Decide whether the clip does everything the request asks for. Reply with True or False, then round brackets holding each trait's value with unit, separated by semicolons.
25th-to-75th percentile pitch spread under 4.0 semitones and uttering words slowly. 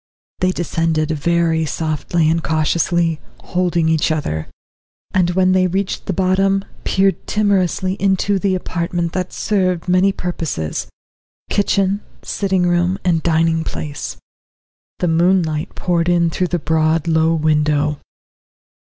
True (2.6 semitones; 125 wpm)